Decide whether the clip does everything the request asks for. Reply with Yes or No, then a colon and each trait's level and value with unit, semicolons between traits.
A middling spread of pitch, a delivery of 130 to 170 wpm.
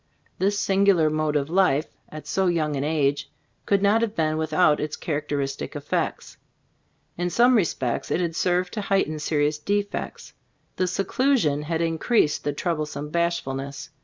Yes: average, 4.4 semitones; average, 155 wpm